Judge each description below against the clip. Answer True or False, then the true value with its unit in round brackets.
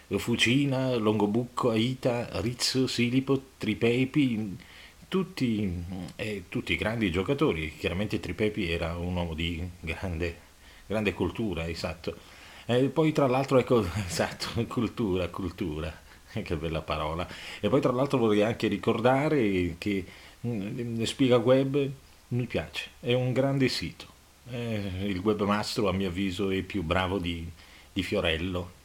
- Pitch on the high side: False (105 Hz)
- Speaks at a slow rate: False (125 wpm)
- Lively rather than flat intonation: True (5.7 semitones)